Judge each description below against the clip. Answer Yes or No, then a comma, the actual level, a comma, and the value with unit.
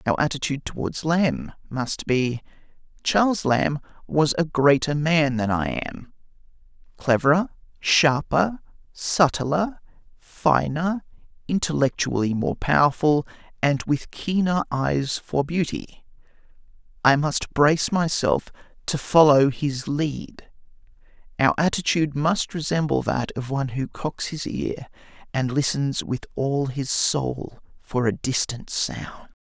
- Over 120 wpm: No, slow, 115 wpm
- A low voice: No, medium, 145 Hz